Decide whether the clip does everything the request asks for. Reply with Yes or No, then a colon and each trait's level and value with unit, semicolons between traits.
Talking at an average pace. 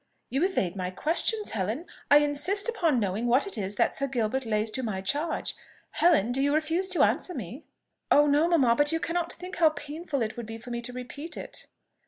No: fast, 215 wpm